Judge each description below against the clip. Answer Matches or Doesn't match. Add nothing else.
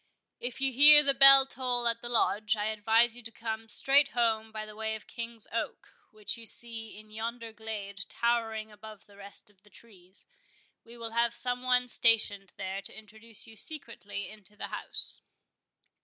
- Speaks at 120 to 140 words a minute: Doesn't match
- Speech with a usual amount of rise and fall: Doesn't match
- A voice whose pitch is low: Doesn't match